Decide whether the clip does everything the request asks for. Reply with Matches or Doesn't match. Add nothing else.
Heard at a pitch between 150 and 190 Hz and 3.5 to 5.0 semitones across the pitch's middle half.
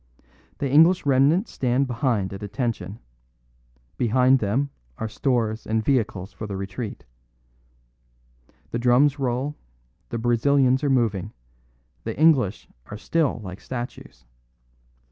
Doesn't match